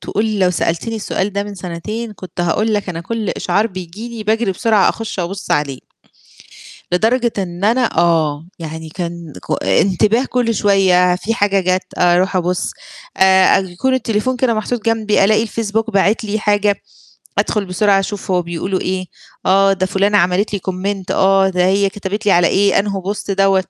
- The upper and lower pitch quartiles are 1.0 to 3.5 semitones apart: Yes, average, 2.9 semitones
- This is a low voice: No, high, 195 Hz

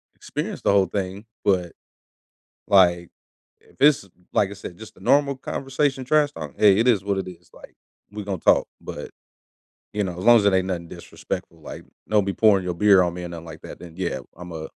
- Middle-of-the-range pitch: No, very low, 95 Hz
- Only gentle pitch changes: No, average, 3.3 semitones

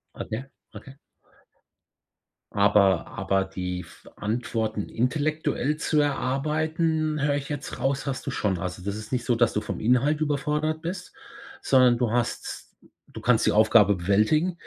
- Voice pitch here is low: Yes, low, 125 Hz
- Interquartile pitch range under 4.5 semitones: No, wide, 6.1 semitones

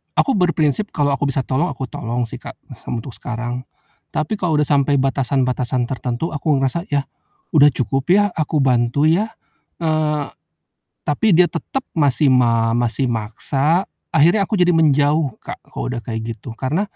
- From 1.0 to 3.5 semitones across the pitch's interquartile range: No, average, 4.3 semitones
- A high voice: No, medium, 140 Hz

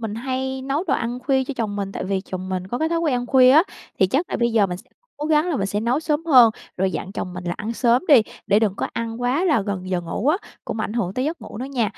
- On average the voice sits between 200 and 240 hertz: Yes, high, 235 Hz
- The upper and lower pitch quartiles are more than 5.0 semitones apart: Yes, wide, 5.5 semitones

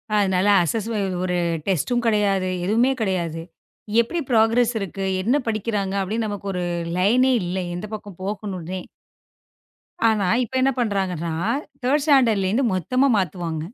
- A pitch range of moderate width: Yes, average, 3.7 semitones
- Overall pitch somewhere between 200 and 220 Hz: Yes, high, 205 Hz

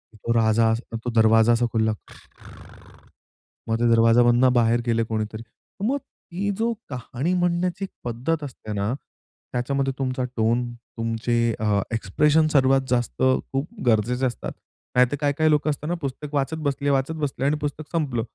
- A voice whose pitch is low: Yes, low, 125 Hz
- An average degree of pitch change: Yes, average, 4.3 semitones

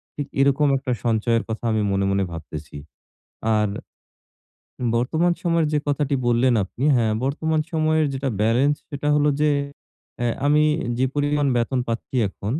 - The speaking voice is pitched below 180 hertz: Yes, low, 135 Hz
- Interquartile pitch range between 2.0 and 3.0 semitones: No, average, 4.4 semitones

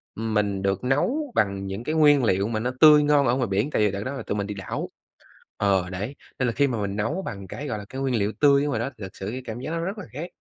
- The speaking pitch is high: No, low, 115 Hz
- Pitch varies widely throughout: Yes, wide, 6.1 semitones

